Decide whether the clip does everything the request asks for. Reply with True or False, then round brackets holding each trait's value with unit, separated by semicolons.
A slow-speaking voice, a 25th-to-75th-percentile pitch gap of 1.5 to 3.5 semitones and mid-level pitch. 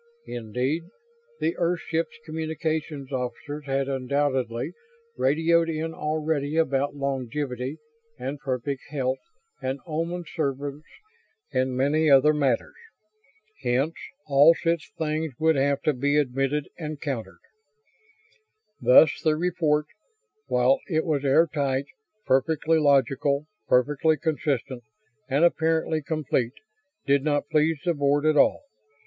True (115 wpm; 2.8 semitones; 145 Hz)